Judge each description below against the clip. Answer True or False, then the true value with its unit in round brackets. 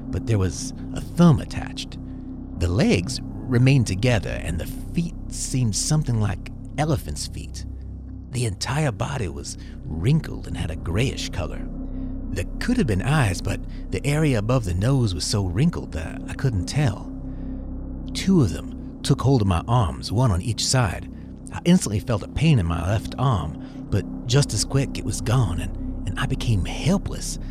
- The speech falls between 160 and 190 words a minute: True (170 wpm)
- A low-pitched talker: True (110 Hz)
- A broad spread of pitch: True (6.8 semitones)